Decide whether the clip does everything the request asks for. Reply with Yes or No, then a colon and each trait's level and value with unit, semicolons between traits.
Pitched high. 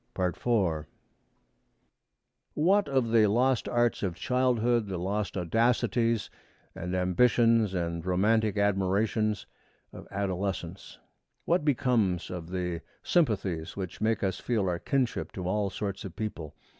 No: low, 100 Hz